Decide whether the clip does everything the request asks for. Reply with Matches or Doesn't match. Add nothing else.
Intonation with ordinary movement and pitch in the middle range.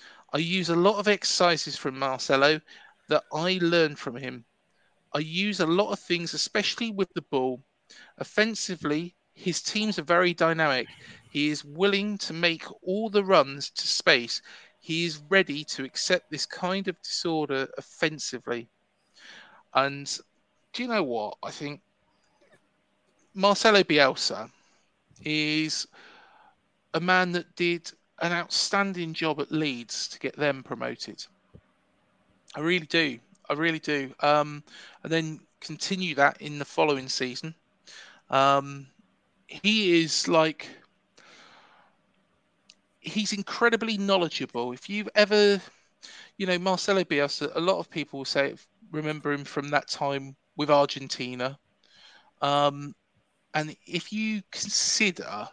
Matches